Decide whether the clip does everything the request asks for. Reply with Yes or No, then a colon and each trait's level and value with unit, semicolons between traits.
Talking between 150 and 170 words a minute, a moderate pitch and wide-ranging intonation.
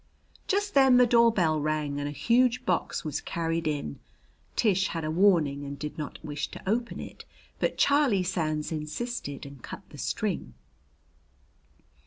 Yes: average, 155 wpm; medium, 165 Hz; wide, 7.8 semitones